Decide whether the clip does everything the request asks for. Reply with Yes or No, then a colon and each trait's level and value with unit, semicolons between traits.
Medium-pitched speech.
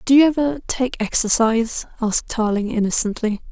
No: high, 235 Hz